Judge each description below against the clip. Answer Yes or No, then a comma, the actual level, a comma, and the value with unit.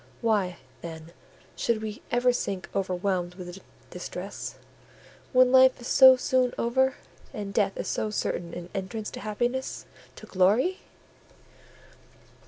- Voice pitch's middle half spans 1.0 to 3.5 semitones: No, average, 5.1 semitones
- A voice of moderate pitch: No, high, 215 Hz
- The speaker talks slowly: Yes, slow, 120 wpm